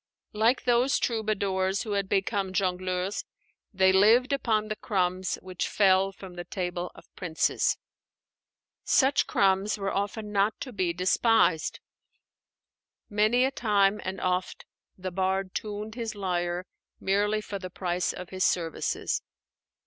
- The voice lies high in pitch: Yes, high, 195 Hz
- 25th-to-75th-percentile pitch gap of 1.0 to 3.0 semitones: Yes, narrow, 2.5 semitones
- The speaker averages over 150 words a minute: No, slow, 135 wpm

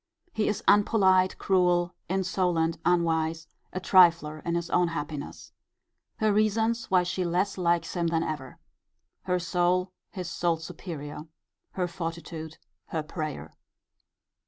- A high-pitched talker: No, medium, 175 Hz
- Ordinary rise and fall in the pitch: No, narrow, 2.3 semitones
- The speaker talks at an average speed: No, slow, 125 wpm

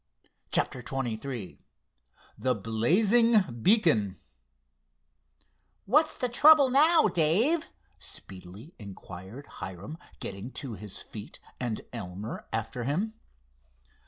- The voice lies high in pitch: No, low, 125 Hz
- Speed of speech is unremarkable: No, slow, 90 wpm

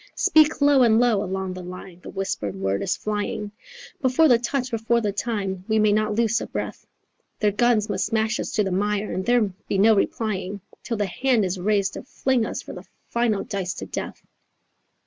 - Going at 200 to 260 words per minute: Yes, fast, 205 wpm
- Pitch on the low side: No, high, 210 Hz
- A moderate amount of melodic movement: Yes, average, 3.4 semitones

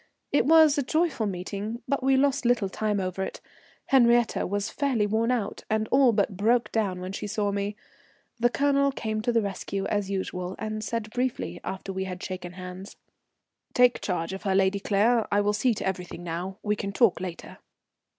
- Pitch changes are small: No, average, 3.9 semitones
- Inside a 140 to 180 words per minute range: No, average, 190 wpm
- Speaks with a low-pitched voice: No, high, 210 Hz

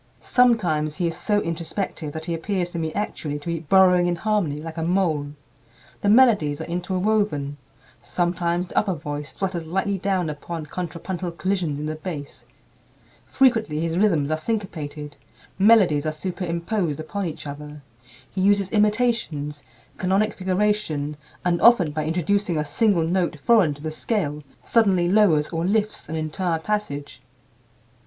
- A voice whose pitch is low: No, medium, 175 Hz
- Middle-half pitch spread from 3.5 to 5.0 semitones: Yes, average, 4.5 semitones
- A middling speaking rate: Yes, average, 150 wpm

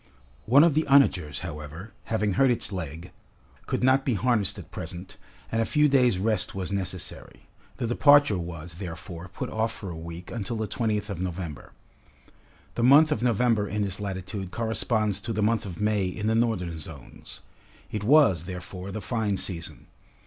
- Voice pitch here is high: No, low, 100 Hz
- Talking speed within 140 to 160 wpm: No, average, 175 wpm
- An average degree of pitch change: Yes, average, 4.2 semitones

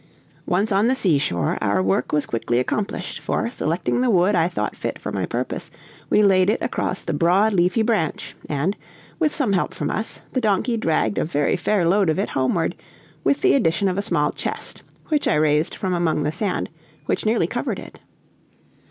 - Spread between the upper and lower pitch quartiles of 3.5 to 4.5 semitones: No, wide, 5.5 semitones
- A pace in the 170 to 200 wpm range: Yes, average, 195 wpm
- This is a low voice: No, medium, 185 Hz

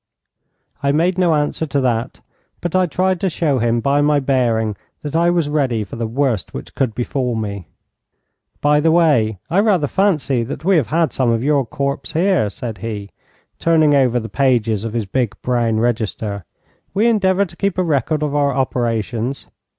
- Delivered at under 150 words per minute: No, average, 185 wpm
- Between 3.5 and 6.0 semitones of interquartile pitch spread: Yes, wide, 5.6 semitones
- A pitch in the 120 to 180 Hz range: Yes, medium, 140 Hz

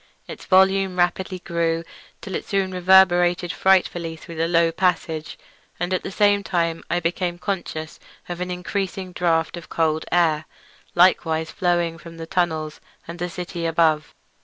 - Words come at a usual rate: Yes, average, 155 wpm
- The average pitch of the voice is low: No, medium, 175 Hz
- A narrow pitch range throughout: Yes, narrow, 2.0 semitones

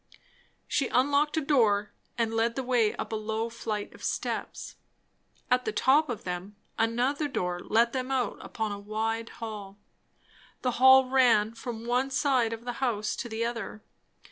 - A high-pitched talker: Yes, high, 230 Hz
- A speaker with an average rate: Yes, average, 170 wpm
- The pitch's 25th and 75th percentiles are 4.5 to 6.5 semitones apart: No, average, 3.0 semitones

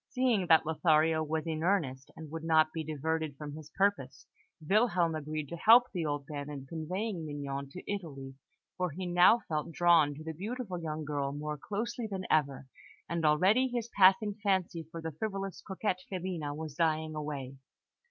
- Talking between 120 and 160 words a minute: No, average, 175 wpm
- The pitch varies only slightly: No, average, 3.8 semitones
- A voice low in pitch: No, medium, 160 Hz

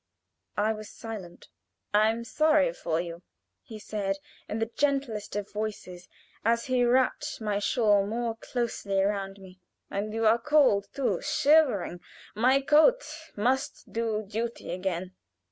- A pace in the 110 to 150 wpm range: Yes, average, 140 wpm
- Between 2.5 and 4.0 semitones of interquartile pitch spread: Yes, average, 3.6 semitones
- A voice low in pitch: No, high, 220 Hz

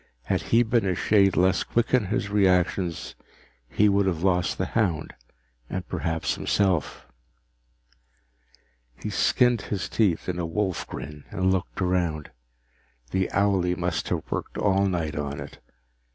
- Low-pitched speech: Yes, very low, 95 Hz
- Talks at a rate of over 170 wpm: No, average, 145 wpm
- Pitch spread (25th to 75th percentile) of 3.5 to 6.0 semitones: No, narrow, 2.5 semitones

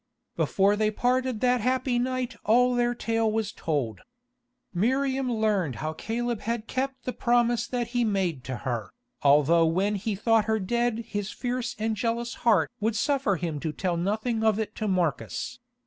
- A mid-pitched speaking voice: No, high, 220 Hz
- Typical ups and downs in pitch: Yes, average, 4.1 semitones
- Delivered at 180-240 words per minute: No, average, 170 wpm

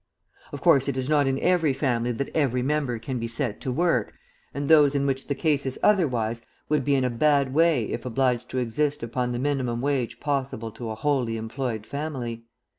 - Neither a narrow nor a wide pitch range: Yes, average, 3.3 semitones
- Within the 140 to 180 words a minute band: No, fast, 205 wpm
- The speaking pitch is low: Yes, low, 130 Hz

